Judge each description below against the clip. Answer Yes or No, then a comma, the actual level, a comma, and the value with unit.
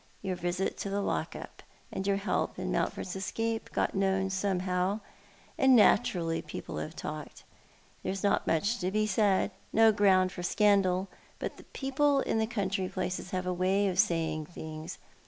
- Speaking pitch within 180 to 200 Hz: Yes, high, 190 Hz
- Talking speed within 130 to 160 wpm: No, average, 175 wpm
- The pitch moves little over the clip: Yes, narrow, 2.3 semitones